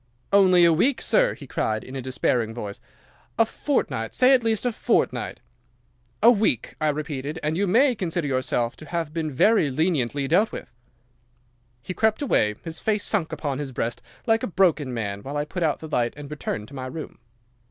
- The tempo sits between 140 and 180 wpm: No, average, 190 wpm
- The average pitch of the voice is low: No, medium, 155 Hz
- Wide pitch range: Yes, wide, 7.4 semitones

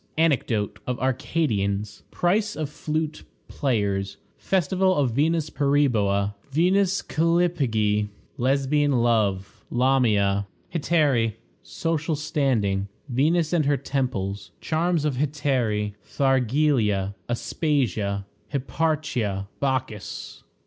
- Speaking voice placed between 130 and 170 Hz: Yes, low, 135 Hz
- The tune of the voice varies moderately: No, wide, 6.6 semitones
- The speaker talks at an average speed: No, slow, 85 wpm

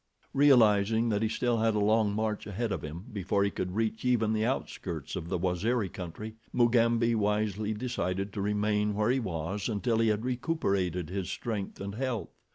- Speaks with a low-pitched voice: Yes, low, 105 Hz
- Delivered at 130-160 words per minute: No, average, 180 wpm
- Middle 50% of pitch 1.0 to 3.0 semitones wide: Yes, average, 2.7 semitones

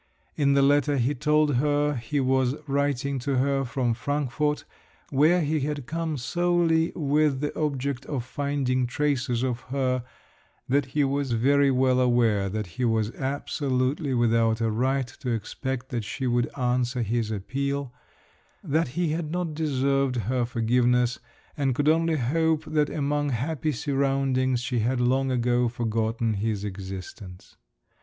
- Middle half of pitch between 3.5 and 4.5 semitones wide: No, average, 3.1 semitones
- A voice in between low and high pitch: No, low, 130 Hz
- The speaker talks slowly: No, average, 150 wpm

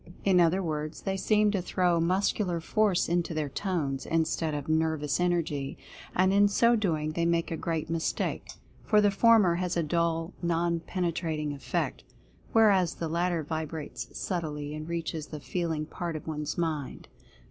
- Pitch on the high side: No, medium, 170 Hz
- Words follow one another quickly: No, average, 165 wpm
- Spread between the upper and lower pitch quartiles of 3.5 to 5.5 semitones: No, average, 2.7 semitones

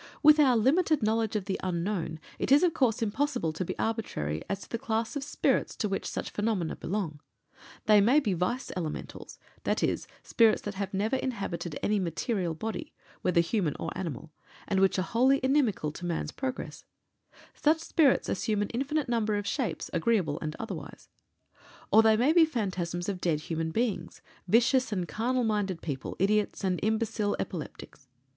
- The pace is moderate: Yes, average, 170 wpm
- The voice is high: Yes, high, 210 Hz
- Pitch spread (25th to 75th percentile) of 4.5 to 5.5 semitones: Yes, average, 5.2 semitones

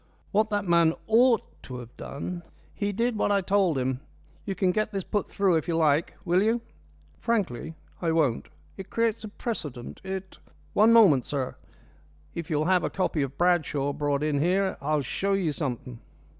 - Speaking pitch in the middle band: Yes, medium, 175 Hz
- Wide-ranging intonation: Yes, wide, 5.7 semitones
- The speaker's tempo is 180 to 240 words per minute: Yes, average, 185 wpm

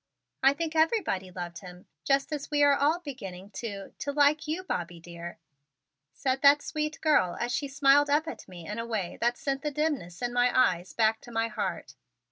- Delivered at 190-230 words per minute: Yes, average, 200 wpm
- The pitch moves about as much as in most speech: No, wide, 7.2 semitones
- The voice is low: No, very high, 260 Hz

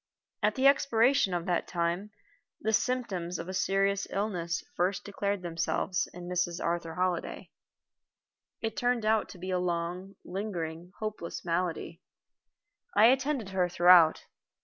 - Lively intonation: No, average, 3.6 semitones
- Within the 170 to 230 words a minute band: No, slow, 135 wpm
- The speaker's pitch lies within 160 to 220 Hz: Yes, medium, 185 Hz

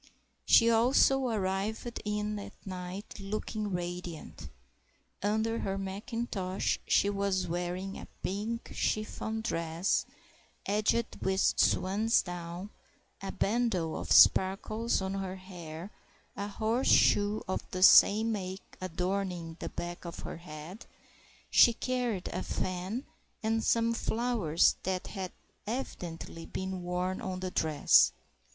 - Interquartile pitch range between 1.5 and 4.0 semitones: Yes, average, 3.4 semitones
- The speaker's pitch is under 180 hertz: No, high, 195 Hz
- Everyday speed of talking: No, slow, 120 wpm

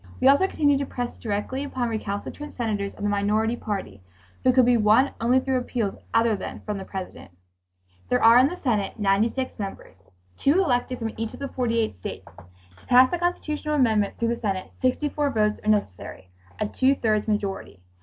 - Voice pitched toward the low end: No, high, 230 Hz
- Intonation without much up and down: No, average, 4.0 semitones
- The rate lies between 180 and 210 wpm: Yes, average, 185 wpm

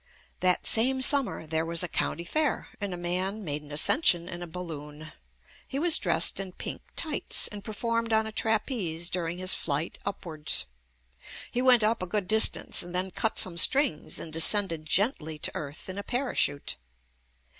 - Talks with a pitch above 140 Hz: Yes, medium, 185 Hz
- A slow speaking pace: No, average, 175 wpm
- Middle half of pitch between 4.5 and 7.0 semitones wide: Yes, average, 5.2 semitones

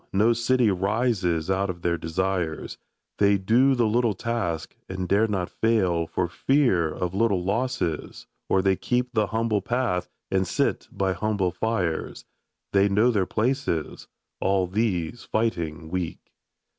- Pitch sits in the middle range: No, low, 100 Hz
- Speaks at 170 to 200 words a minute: No, average, 150 wpm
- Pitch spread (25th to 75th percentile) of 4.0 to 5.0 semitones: Yes, average, 4.3 semitones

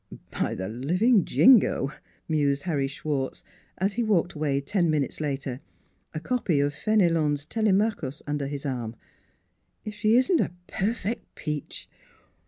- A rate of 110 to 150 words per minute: Yes, average, 145 wpm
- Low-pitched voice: No, medium, 155 Hz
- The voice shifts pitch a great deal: Yes, wide, 6.8 semitones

